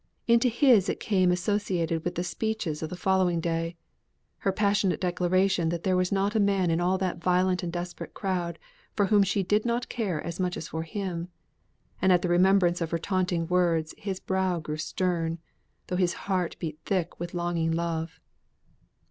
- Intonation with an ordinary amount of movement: No, narrow, 2.2 semitones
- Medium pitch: Yes, medium, 180 Hz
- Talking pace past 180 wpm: Yes, average, 190 wpm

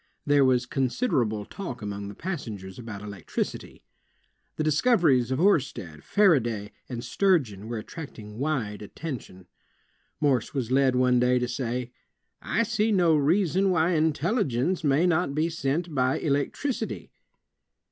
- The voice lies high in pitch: No, low, 135 Hz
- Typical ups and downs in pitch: No, wide, 6.0 semitones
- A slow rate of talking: Yes, slow, 130 wpm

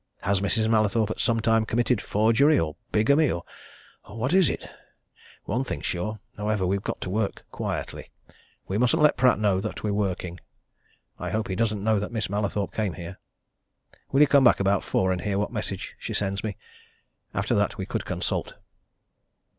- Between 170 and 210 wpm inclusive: Yes, average, 180 wpm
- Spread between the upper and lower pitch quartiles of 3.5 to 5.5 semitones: No, average, 2.8 semitones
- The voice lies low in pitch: Yes, low, 105 Hz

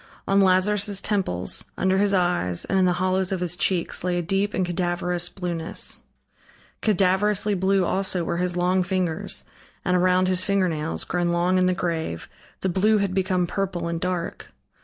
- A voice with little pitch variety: Yes, narrow, 1.5 semitones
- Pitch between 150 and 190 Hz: Yes, medium, 185 Hz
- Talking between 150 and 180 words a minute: Yes, average, 170 wpm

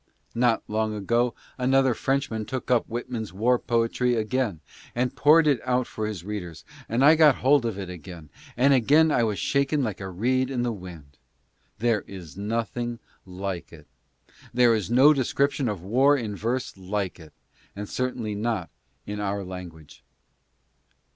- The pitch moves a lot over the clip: No, average, 4.5 semitones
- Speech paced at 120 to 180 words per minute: Yes, average, 160 wpm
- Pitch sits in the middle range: No, low, 115 Hz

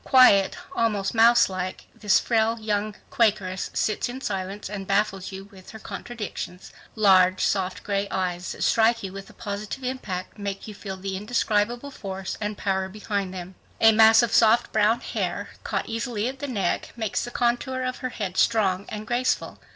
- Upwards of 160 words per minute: Yes, average, 175 wpm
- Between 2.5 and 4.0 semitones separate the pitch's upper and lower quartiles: Yes, average, 3.1 semitones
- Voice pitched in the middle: No, high, 210 Hz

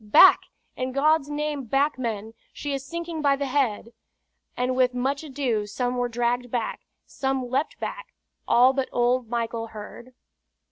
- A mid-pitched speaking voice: No, very high, 255 Hz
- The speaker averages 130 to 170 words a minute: Yes, average, 155 wpm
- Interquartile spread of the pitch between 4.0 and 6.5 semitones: No, average, 2.8 semitones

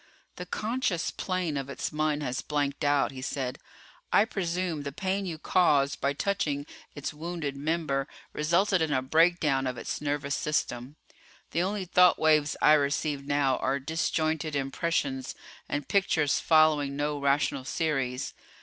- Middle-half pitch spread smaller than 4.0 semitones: Yes, average, 3.1 semitones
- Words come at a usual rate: Yes, average, 150 wpm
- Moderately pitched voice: Yes, medium, 150 Hz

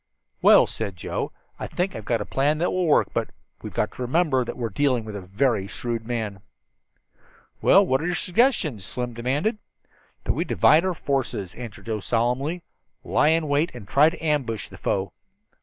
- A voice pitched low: Yes, low, 130 Hz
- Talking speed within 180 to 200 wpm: Yes, average, 190 wpm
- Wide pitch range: Yes, wide, 5.8 semitones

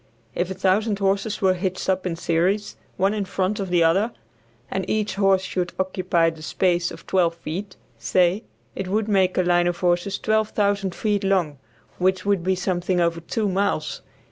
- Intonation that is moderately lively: No, narrow, 2.1 semitones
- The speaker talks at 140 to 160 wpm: No, average, 175 wpm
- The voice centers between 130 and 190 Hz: Yes, medium, 185 Hz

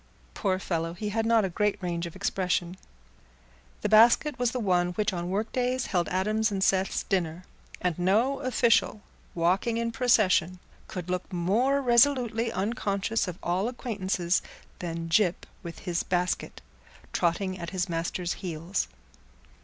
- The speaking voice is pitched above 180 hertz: Yes, high, 190 Hz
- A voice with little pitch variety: No, average, 4.2 semitones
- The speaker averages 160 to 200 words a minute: No, average, 145 wpm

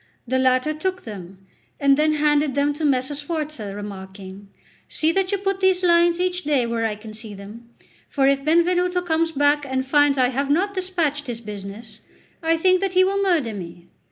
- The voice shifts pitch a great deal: Yes, wide, 6.9 semitones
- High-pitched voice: Yes, very high, 290 Hz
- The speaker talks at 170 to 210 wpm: Yes, average, 190 wpm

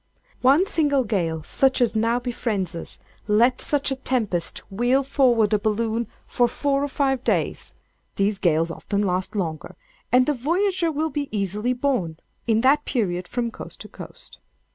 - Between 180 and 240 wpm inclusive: No, average, 160 wpm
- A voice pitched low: No, high, 240 Hz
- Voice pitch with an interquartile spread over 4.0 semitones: Yes, average, 5.2 semitones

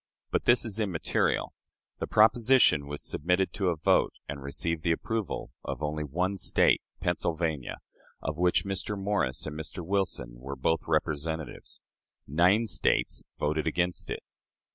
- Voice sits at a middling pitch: No, very low, 85 Hz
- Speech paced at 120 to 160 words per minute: Yes, average, 140 wpm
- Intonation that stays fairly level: No, average, 4.3 semitones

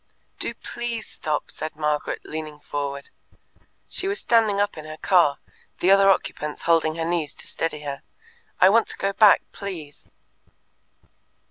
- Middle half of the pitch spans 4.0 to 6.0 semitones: Yes, average, 4.7 semitones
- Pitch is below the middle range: No, medium, 165 Hz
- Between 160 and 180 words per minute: No, average, 150 wpm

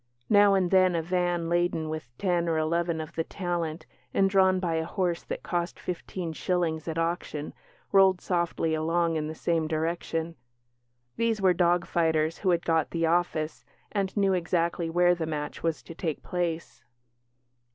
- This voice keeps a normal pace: Yes, average, 170 wpm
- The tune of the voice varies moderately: No, narrow, 1.8 semitones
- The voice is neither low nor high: Yes, medium, 170 Hz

